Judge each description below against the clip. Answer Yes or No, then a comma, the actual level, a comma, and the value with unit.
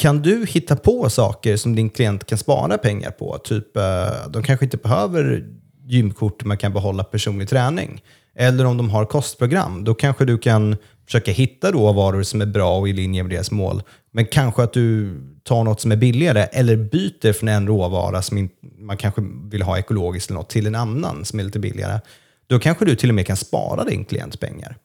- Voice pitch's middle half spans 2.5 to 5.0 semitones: Yes, average, 3.7 semitones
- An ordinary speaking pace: No, fast, 200 wpm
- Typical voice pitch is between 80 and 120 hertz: Yes, low, 110 Hz